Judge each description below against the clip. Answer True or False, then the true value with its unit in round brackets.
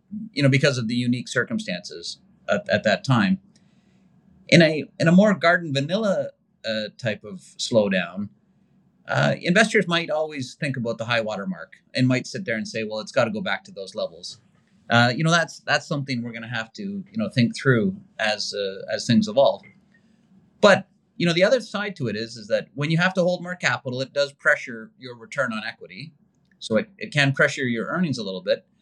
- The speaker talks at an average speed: False (210 wpm)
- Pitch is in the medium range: True (160 Hz)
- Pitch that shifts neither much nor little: False (8.4 semitones)